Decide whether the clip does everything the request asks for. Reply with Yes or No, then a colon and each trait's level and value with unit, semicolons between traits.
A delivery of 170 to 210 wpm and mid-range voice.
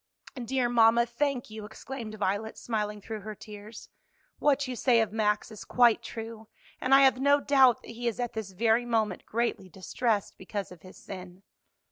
No: average, 180 wpm; high, 225 Hz